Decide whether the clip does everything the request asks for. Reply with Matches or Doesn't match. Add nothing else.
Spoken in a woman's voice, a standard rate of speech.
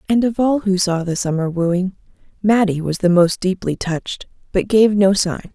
Matches